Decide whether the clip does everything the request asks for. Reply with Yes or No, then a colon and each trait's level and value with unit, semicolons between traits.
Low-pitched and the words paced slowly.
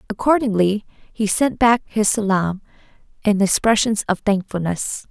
No: high, 210 Hz; slow, 115 wpm